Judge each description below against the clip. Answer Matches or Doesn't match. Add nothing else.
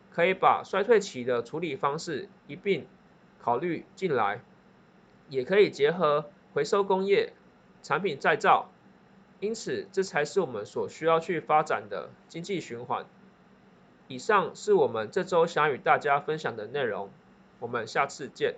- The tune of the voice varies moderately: Doesn't match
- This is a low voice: Doesn't match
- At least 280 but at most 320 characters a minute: Doesn't match